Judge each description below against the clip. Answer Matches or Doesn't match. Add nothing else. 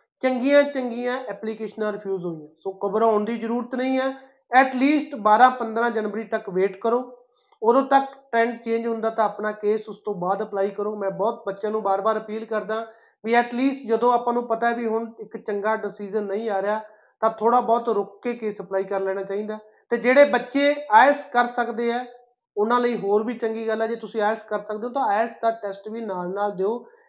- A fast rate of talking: Matches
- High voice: Matches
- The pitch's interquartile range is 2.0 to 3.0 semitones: Matches